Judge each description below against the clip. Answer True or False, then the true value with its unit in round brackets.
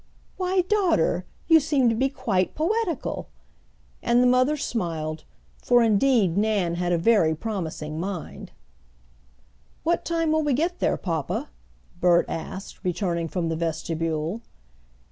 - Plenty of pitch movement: True (9.0 semitones)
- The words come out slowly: True (130 wpm)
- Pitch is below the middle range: False (205 Hz)